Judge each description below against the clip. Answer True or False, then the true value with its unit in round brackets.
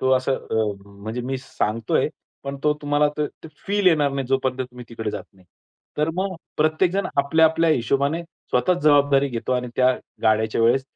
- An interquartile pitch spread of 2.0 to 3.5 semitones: False (4.2 semitones)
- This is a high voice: False (135 Hz)